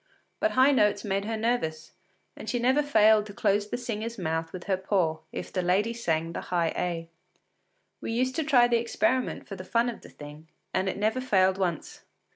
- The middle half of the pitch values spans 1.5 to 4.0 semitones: No, average, 5.0 semitones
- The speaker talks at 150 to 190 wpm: No, fast, 205 wpm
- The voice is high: Yes, high, 210 Hz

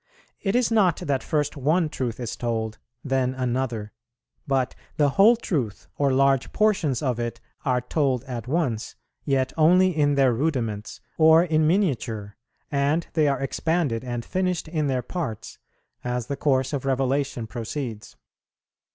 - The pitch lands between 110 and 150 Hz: Yes, low, 135 Hz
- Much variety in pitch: No, average, 4.3 semitones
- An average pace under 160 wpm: Yes, average, 150 wpm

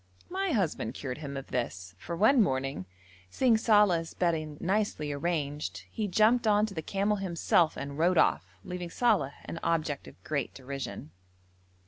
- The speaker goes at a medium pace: Yes, average, 155 wpm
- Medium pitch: Yes, medium, 170 Hz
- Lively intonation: Yes, wide, 6.6 semitones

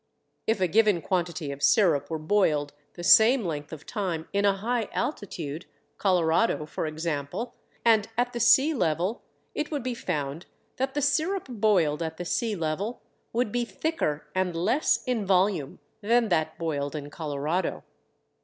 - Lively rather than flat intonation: Yes, wide, 6.5 semitones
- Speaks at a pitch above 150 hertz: Yes, medium, 185 Hz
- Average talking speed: Yes, average, 160 wpm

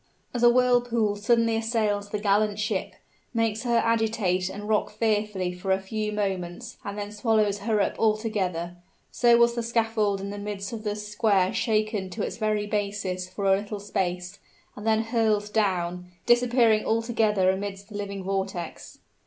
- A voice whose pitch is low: No, high, 210 Hz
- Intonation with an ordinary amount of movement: No, narrow, 2.2 semitones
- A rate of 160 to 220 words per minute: Yes, average, 165 wpm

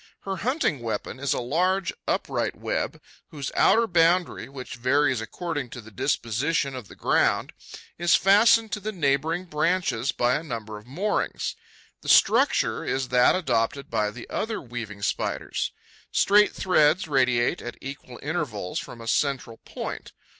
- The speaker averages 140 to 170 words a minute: Yes, average, 150 wpm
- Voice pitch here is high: No, medium, 140 Hz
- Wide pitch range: Yes, wide, 6.5 semitones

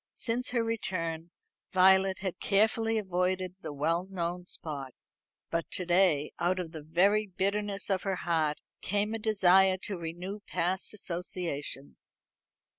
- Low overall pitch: No, medium, 185 Hz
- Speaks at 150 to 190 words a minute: No, slow, 135 wpm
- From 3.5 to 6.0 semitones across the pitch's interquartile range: No, average, 2.9 semitones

